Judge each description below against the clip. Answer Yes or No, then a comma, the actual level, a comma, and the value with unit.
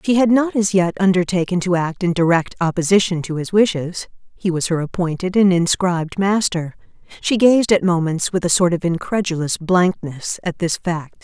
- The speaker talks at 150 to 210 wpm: Yes, average, 180 wpm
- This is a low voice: No, medium, 180 Hz